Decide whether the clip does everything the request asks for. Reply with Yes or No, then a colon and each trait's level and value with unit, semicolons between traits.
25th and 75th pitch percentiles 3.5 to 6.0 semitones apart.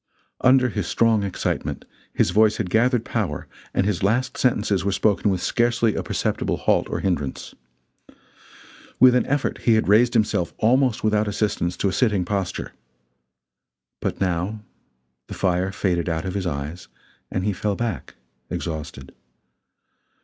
Yes: average, 3.9 semitones